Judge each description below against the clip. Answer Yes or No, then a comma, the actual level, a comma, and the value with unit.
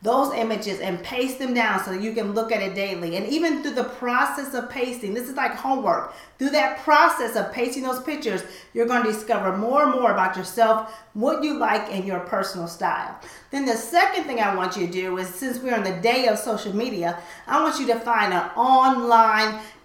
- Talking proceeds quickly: Yes, fast, 220 wpm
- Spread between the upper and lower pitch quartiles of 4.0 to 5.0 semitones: Yes, average, 4.3 semitones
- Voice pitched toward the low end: No, high, 230 Hz